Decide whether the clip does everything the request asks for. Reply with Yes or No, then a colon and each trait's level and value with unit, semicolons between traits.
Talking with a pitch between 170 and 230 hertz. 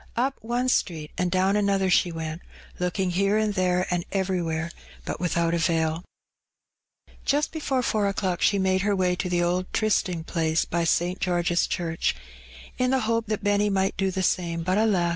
Yes: medium, 185 Hz